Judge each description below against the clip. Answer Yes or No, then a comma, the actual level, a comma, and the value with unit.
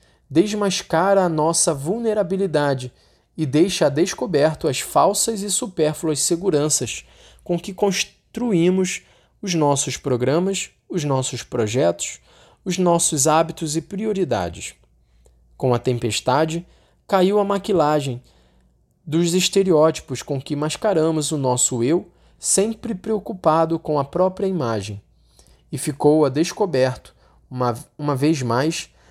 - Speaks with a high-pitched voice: No, medium, 155 Hz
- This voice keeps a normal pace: No, slow, 115 wpm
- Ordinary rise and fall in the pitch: No, wide, 6.3 semitones